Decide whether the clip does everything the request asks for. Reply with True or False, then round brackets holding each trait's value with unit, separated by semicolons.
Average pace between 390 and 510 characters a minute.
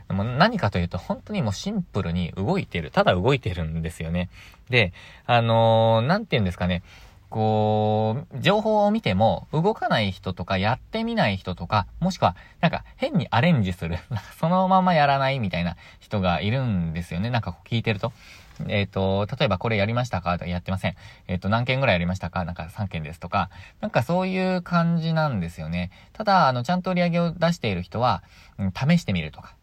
True (415 characters per minute)